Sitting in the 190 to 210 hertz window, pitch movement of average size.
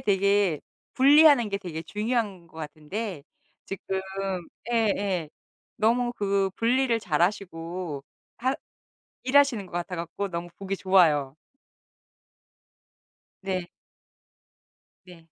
Yes: high, 195 Hz; average, 4.8 semitones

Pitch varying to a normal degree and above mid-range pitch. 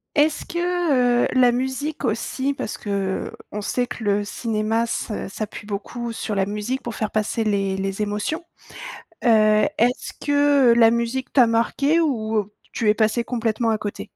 Yes: average, 3.1 semitones; high, 230 Hz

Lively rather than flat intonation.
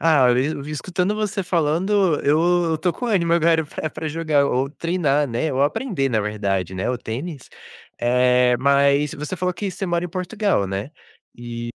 Yes: wide, 5.7 semitones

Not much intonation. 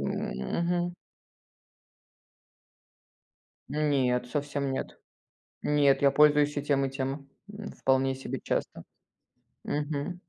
Yes: narrow, 1.9 semitones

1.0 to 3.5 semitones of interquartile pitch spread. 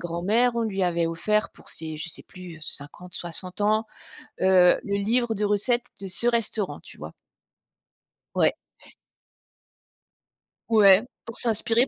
No: average, 4.1 semitones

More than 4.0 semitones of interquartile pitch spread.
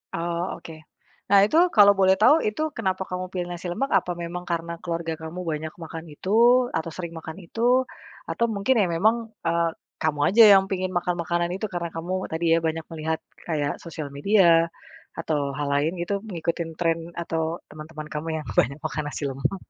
No: narrow, 2.6 semitones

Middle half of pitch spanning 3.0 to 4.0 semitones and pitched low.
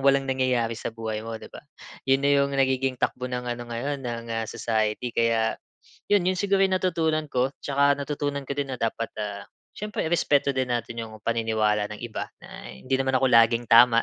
Yes: average, 3.5 semitones; low, 125 Hz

